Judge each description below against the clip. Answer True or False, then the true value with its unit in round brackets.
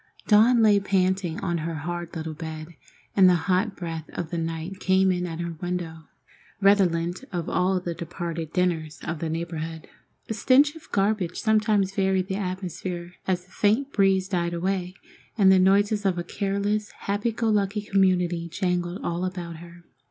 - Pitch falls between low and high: True (180 Hz)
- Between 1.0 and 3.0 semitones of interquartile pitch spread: True (2.6 semitones)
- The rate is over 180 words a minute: False (170 wpm)